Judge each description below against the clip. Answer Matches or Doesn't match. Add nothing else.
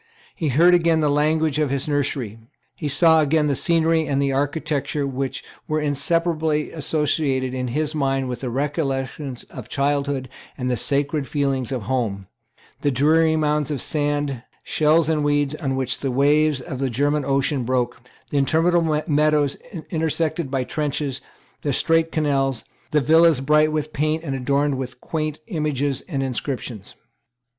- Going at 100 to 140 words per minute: Doesn't match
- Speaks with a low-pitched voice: Doesn't match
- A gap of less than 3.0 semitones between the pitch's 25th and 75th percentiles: Matches